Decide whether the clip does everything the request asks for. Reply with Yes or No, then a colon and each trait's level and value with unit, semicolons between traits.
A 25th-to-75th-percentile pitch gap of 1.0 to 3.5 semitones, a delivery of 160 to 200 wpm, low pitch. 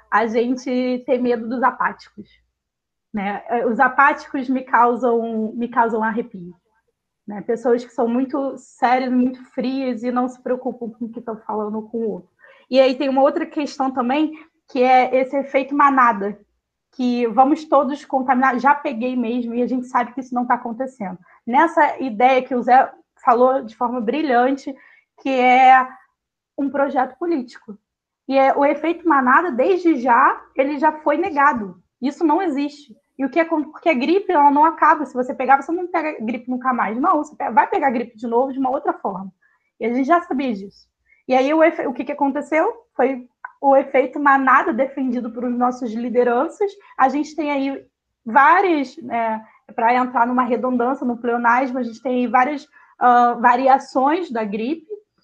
No: average, 2.9 semitones; average, 175 wpm; very high, 260 Hz